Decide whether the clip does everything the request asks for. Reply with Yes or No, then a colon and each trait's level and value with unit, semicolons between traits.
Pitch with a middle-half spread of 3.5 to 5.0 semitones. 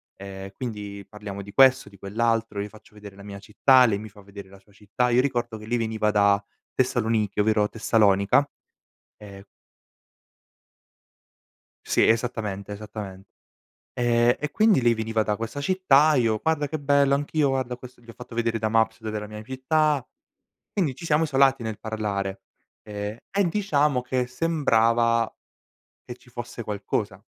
Yes: average, 3.9 semitones